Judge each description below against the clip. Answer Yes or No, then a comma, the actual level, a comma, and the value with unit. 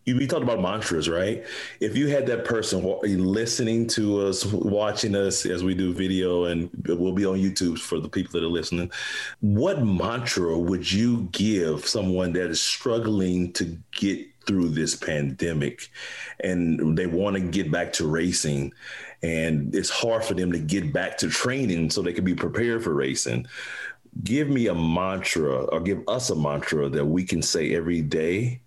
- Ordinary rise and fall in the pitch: Yes, average, 3.6 semitones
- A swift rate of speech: No, average, 175 wpm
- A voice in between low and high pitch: No, very low, 90 Hz